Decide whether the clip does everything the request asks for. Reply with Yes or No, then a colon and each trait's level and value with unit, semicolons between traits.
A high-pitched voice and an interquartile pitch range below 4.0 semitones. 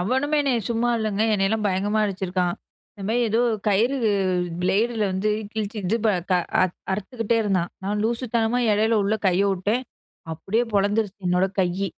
Yes: high, 210 Hz; average, 3.0 semitones